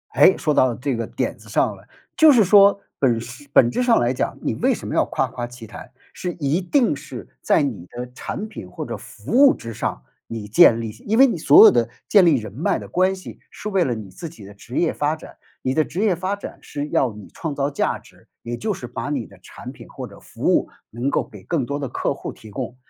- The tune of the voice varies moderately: No, wide, 7.7 semitones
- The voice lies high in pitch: No, medium, 140 Hz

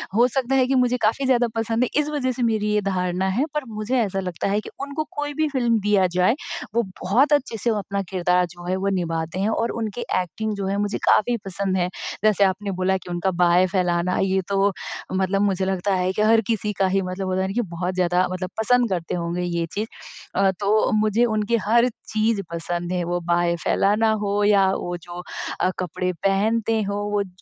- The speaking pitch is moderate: No, high, 200 Hz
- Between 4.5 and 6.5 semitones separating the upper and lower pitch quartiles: No, average, 3.6 semitones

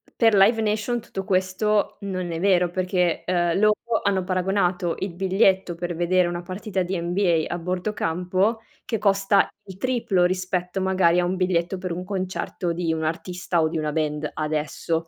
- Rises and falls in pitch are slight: Yes, narrow, 2.0 semitones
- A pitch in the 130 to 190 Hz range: Yes, medium, 185 Hz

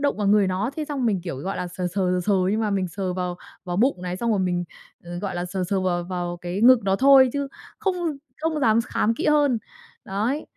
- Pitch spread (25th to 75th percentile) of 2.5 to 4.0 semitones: No, average, 5.3 semitones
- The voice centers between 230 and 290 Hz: No, high, 195 Hz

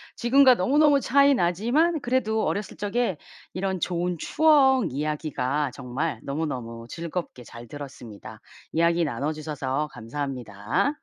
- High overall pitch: No, medium, 165 Hz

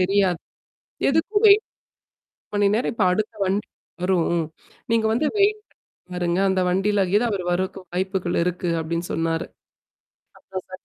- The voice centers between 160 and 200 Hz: Yes, high, 190 Hz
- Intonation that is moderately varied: Yes, average, 3.3 semitones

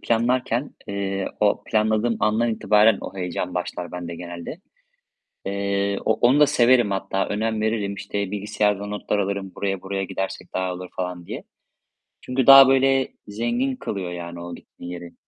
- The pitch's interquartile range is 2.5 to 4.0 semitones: Yes, average, 3.2 semitones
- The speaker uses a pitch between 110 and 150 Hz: No, low, 100 Hz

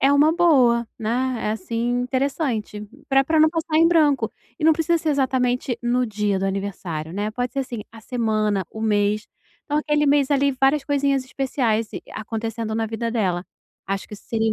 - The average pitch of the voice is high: Yes, high, 245 Hz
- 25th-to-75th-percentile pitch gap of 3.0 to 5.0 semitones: Yes, average, 4.6 semitones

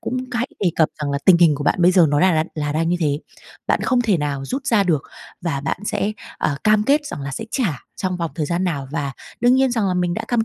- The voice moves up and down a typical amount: No, wide, 6.5 semitones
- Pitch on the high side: No, medium, 175 Hz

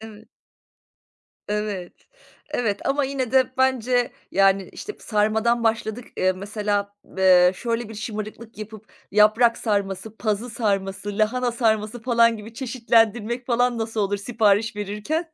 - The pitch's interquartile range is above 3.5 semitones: No, narrow, 2.6 semitones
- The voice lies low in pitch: No, high, 220 Hz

